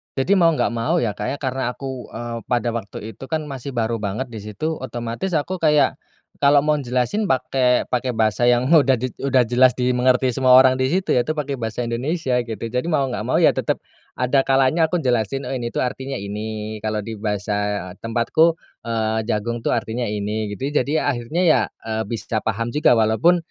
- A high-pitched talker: No, low, 125 Hz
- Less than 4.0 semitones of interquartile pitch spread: Yes, average, 3.4 semitones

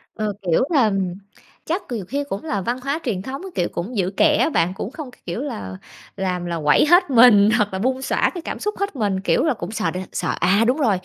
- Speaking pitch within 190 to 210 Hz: No, high, 220 Hz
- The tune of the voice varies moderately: No, wide, 6.7 semitones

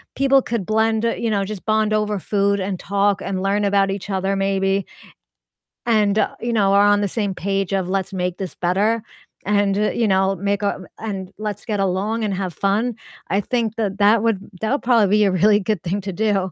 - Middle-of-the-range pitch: No, high, 200 Hz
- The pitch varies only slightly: Yes, narrow, 1.8 semitones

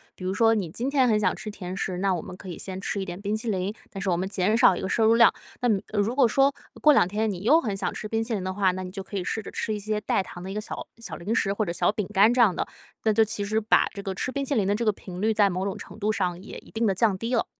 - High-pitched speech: Yes, high, 205 Hz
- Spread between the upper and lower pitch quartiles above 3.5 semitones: No, average, 2.8 semitones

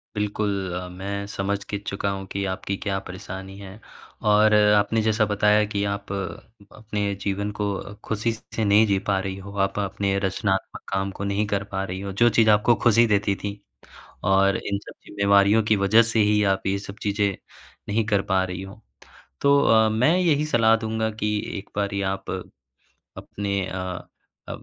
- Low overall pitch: Yes, low, 100 Hz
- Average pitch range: No, narrow, 1.6 semitones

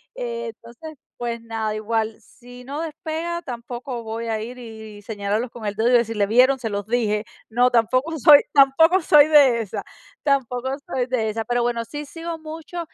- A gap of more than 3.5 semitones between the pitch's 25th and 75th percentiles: Yes, average, 3.9 semitones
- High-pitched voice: Yes, high, 240 Hz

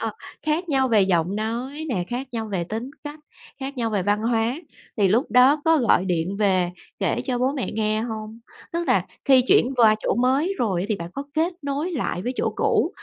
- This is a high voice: Yes, high, 235 Hz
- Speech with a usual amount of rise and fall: Yes, average, 4.6 semitones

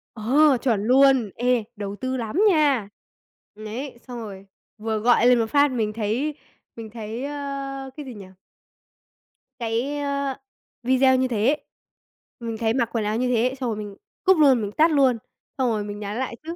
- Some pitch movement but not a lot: Yes, average, 3.8 semitones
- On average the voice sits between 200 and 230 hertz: No, high, 245 Hz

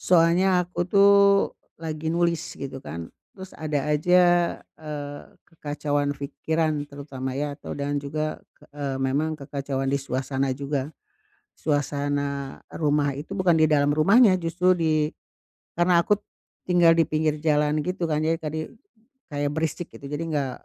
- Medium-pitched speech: Yes, medium, 150 Hz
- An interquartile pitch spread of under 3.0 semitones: Yes, narrow, 2.5 semitones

